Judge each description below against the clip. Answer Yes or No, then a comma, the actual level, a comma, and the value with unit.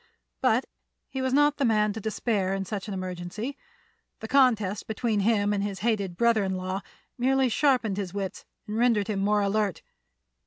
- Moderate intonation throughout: Yes, average, 3.2 semitones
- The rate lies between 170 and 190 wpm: Yes, average, 180 wpm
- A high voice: Yes, high, 210 Hz